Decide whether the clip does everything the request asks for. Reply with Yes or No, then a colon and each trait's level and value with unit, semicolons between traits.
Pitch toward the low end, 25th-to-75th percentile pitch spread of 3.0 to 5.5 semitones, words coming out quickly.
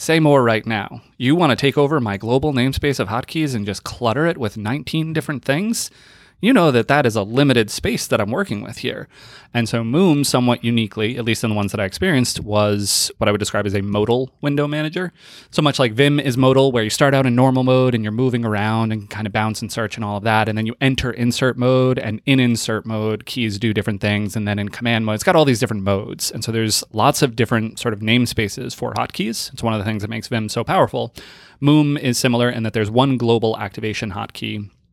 Yes: low, 120 Hz; average, 3.5 semitones; fast, 240 wpm